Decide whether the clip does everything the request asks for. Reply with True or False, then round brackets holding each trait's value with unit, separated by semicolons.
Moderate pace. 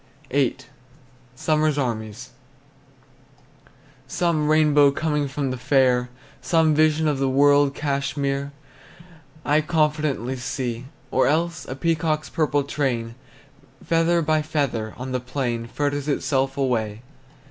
False (115 wpm)